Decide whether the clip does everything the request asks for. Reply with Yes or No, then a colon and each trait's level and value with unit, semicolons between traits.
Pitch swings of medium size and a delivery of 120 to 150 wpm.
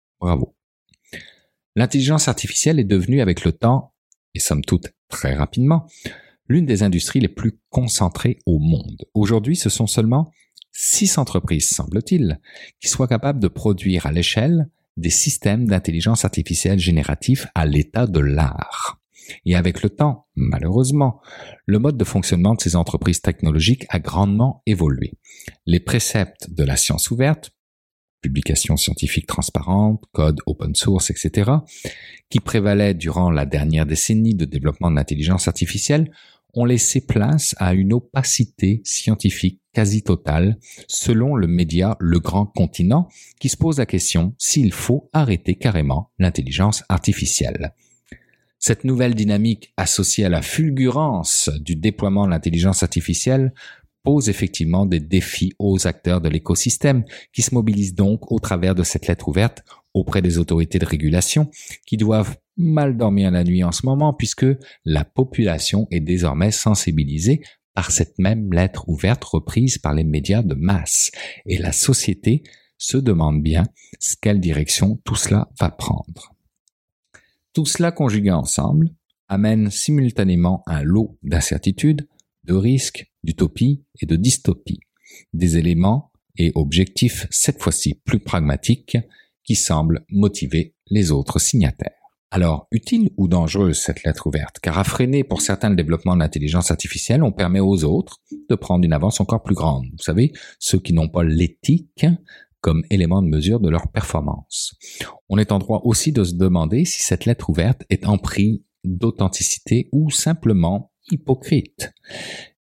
No: wide, 6.0 semitones; slow, 145 wpm